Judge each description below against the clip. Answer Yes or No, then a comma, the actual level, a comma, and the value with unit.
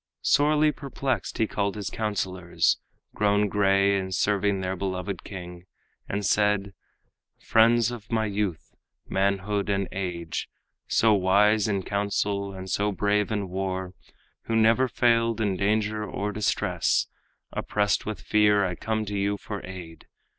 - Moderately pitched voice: No, low, 100 Hz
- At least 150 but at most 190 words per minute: No, average, 140 wpm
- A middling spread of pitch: No, narrow, 1.9 semitones